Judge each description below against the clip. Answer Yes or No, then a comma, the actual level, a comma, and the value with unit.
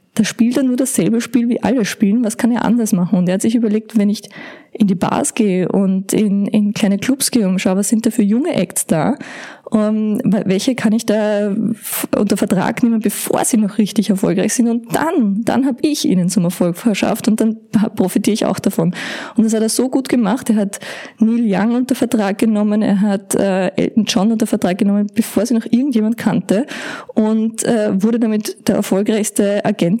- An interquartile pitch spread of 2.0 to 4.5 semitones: Yes, narrow, 2.5 semitones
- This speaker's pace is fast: Yes, fast, 200 wpm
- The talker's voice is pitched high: Yes, high, 220 Hz